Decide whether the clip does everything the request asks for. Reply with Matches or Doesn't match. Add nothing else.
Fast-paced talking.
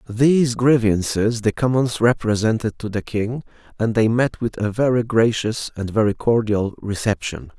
Doesn't match